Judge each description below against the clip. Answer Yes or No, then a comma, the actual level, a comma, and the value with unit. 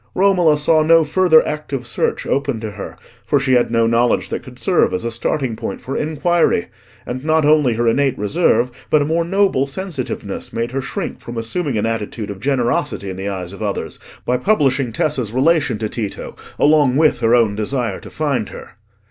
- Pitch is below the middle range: Yes, low, 130 Hz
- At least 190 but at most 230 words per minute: Yes, average, 195 wpm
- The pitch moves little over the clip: No, average, 5.2 semitones